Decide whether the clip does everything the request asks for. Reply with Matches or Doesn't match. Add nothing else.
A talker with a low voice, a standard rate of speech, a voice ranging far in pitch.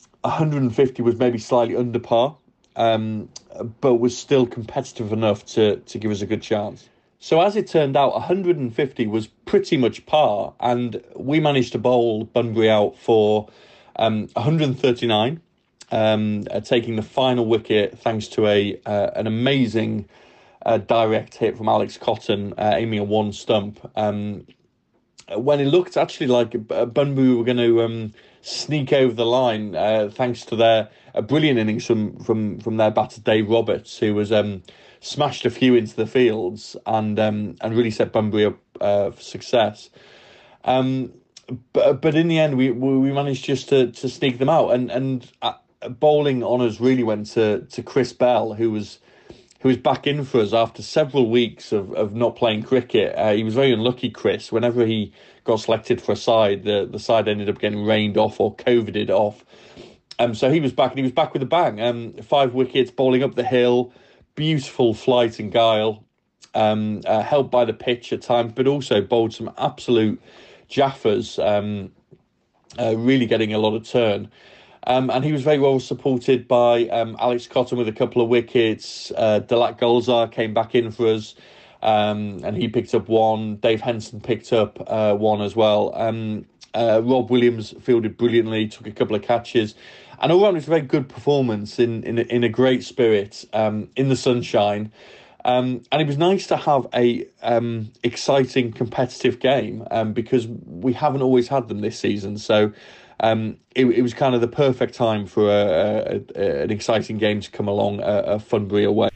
Doesn't match